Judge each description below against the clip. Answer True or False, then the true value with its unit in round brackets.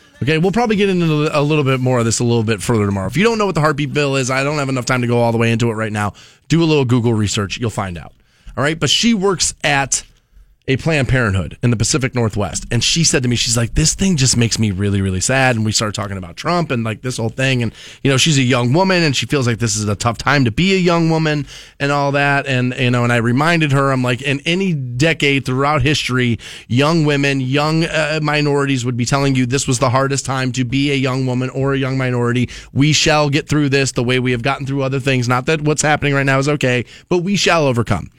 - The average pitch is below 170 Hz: True (135 Hz)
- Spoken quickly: True (270 wpm)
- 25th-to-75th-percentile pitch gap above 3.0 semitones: True (3.7 semitones)